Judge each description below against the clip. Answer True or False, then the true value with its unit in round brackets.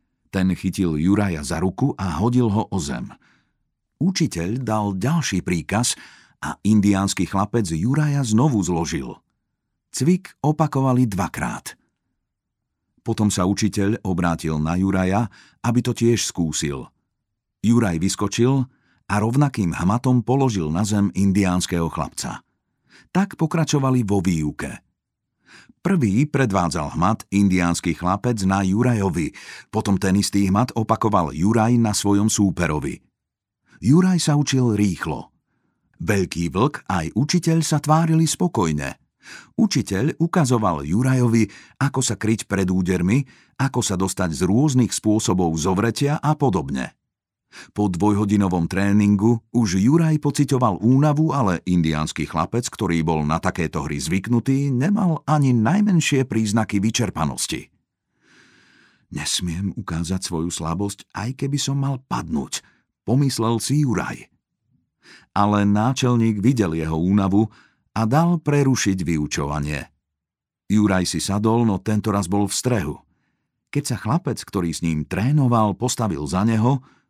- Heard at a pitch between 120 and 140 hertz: False (105 Hz)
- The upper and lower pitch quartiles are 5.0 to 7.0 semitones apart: True (5.6 semitones)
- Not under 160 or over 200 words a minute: False (120 wpm)